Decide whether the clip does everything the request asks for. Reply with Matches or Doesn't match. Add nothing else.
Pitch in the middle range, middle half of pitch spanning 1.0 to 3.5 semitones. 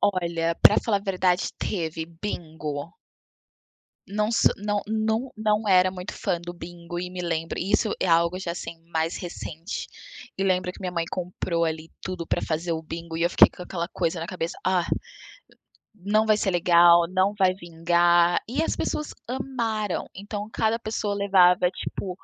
Matches